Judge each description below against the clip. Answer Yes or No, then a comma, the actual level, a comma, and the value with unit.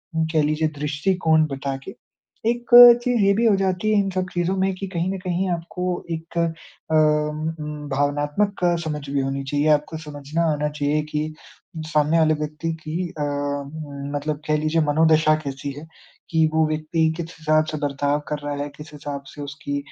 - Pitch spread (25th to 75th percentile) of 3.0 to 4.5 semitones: No, narrow, 2.5 semitones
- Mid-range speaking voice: Yes, medium, 155 Hz